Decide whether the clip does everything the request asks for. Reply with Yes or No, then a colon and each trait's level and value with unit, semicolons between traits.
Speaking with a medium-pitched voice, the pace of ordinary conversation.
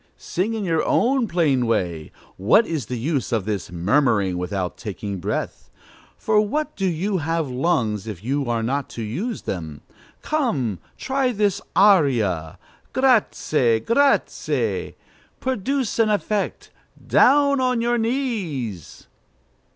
No: medium, 155 Hz; slow, 130 wpm